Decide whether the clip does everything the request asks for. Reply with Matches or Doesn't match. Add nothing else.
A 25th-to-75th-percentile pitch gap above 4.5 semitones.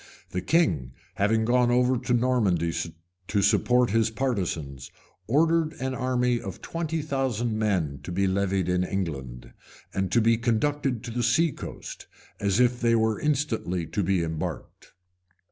Matches